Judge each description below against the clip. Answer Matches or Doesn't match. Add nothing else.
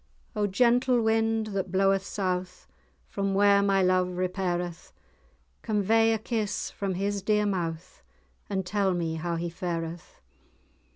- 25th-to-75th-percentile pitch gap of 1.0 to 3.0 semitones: Matches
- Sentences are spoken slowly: Matches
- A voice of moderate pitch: Doesn't match